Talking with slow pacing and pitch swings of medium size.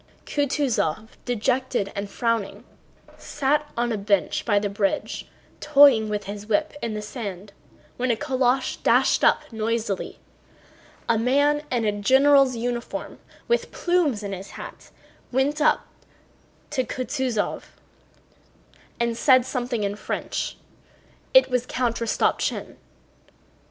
Yes: slow, 120 wpm; average, 4.0 semitones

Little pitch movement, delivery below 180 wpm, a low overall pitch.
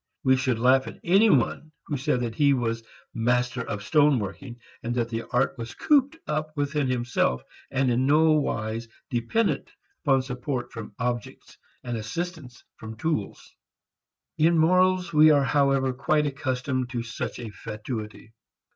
No: average, 4.2 semitones; average, 155 wpm; low, 130 Hz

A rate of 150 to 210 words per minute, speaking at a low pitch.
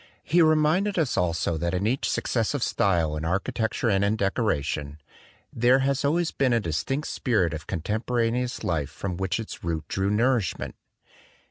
Yes: average, 155 wpm; low, 110 Hz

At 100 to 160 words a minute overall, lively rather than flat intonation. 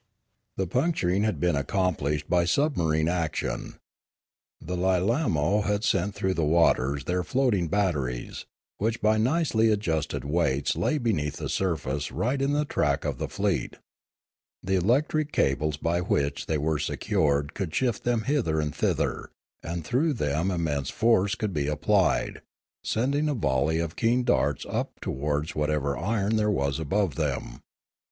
Yes: average, 150 wpm; wide, 6.7 semitones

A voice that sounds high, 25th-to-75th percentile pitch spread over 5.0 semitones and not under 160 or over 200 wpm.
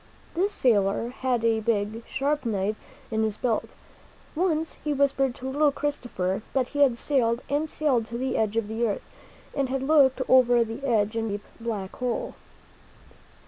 No: high, 245 Hz; average, 3.8 semitones; average, 175 wpm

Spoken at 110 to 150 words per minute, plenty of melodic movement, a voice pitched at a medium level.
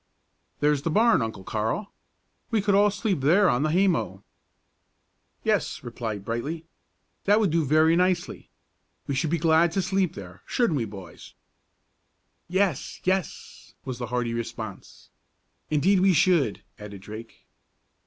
Yes: average, 140 wpm; wide, 8.3 semitones; medium, 155 Hz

